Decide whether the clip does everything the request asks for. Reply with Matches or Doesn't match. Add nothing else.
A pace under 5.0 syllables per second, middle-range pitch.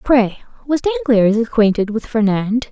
Doesn't match